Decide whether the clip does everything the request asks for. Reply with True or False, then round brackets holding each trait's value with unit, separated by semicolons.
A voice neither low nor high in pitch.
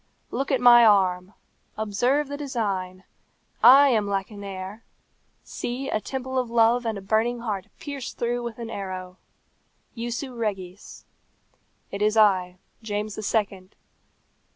False (220 Hz)